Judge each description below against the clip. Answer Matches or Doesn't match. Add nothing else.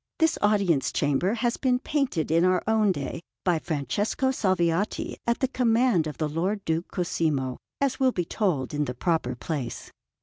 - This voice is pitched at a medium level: Matches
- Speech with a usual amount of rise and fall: Doesn't match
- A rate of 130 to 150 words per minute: Doesn't match